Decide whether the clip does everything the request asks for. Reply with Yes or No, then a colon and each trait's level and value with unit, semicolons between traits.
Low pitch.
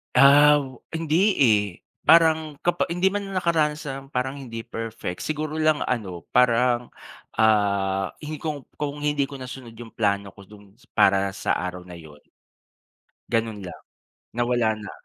Yes: low, 125 Hz